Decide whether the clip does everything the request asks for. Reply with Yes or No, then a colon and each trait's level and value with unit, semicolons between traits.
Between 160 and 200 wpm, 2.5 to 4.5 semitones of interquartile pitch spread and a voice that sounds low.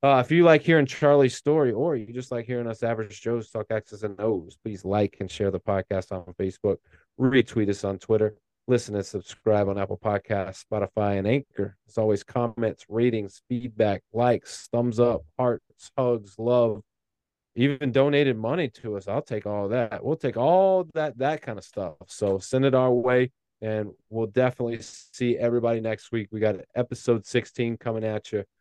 Yes: average, 180 wpm; average, 3.3 semitones; low, 115 Hz